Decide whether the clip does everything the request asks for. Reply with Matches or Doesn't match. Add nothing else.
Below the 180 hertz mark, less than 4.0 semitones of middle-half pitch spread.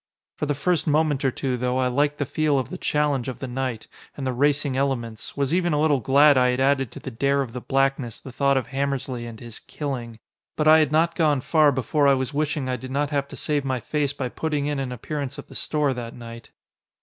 Matches